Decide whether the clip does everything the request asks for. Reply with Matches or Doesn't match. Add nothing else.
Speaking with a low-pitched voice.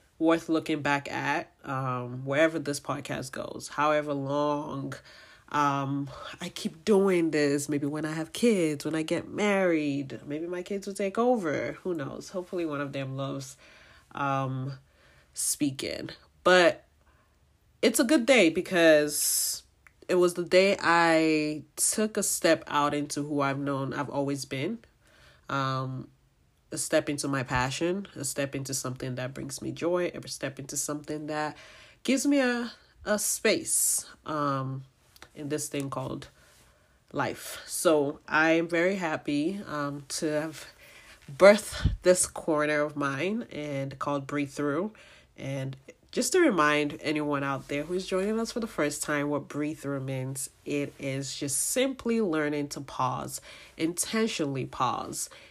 Doesn't match